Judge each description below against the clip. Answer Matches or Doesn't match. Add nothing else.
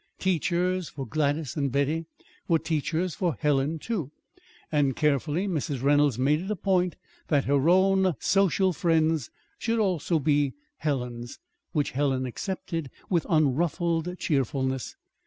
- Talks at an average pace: Doesn't match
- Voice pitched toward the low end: Doesn't match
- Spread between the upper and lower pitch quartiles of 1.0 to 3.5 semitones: Doesn't match